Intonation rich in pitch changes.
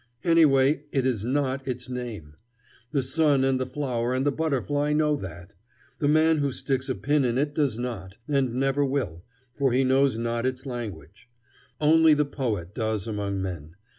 No: average, 3.6 semitones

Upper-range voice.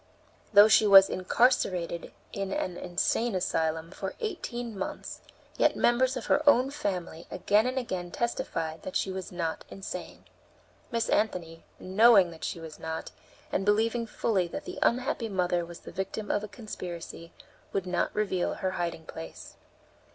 Yes: high, 195 Hz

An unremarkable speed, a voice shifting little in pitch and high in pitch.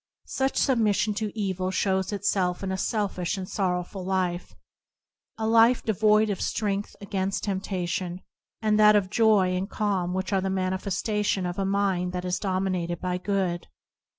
Yes: average, 165 wpm; narrow, 2.3 semitones; high, 195 Hz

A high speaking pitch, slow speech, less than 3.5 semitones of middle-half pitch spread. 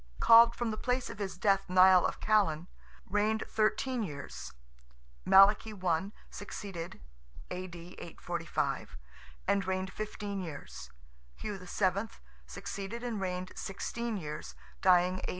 Yes: high, 195 Hz; slow, 120 wpm; average, 2.9 semitones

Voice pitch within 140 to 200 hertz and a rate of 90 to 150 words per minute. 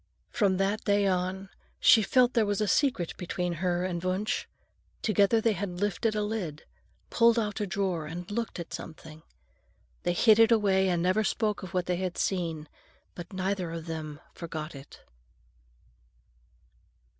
No: high, 190 Hz; average, 160 wpm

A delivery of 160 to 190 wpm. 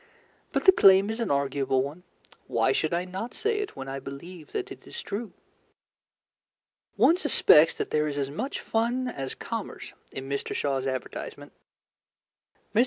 Yes: average, 165 wpm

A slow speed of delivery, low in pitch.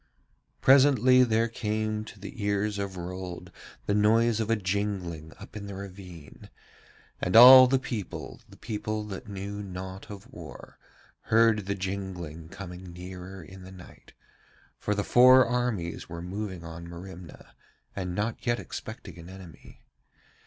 No: average, 145 wpm; low, 100 Hz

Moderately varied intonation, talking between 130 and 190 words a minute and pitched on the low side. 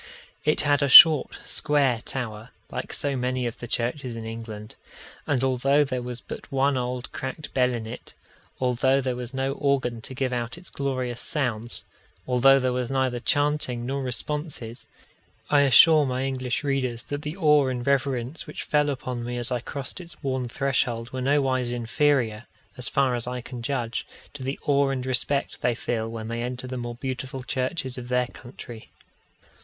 No: narrow, 2.3 semitones; average, 180 wpm; low, 130 Hz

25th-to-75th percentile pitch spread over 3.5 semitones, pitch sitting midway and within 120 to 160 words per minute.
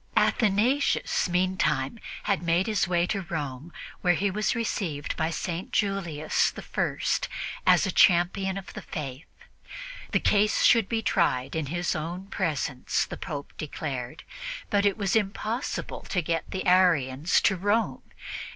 Yes: average, 4.4 semitones; medium, 180 Hz; average, 150 wpm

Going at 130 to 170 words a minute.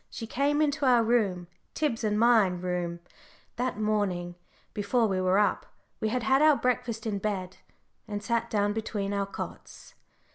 Yes: average, 160 wpm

